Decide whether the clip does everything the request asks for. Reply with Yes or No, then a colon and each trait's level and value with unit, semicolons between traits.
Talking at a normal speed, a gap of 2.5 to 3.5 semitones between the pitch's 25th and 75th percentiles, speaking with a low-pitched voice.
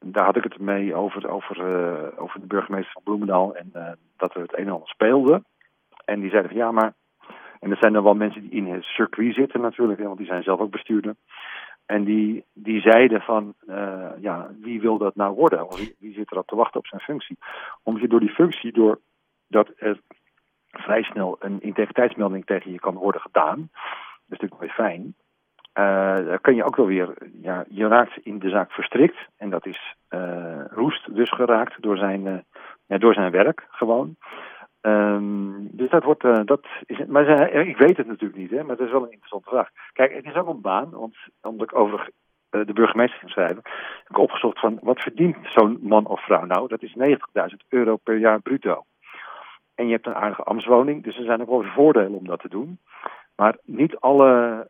No: fast, 210 wpm; average, 2.9 semitones; low, 110 Hz